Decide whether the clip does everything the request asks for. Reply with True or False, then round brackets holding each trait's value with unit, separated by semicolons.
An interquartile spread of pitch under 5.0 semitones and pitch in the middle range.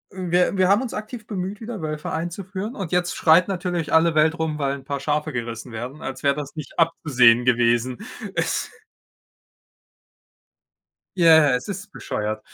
False (5.4 semitones; 160 Hz)